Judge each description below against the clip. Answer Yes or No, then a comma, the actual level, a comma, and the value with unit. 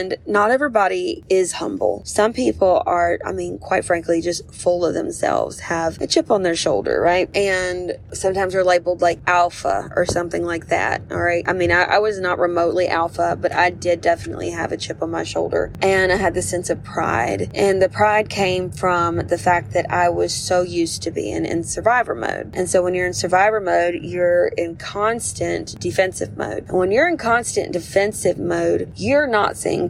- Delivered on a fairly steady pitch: Yes, narrow, 2.0 semitones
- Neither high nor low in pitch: Yes, medium, 180 Hz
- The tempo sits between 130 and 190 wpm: No, average, 200 wpm